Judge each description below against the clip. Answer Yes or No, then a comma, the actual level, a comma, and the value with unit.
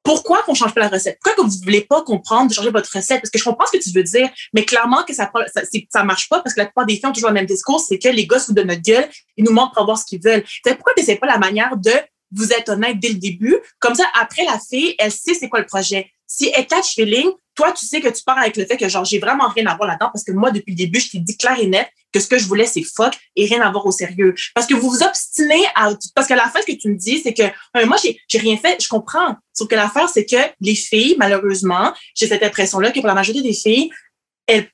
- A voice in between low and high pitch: No, high, 225 Hz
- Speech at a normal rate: No, fast, 300 wpm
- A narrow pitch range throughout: No, average, 4.1 semitones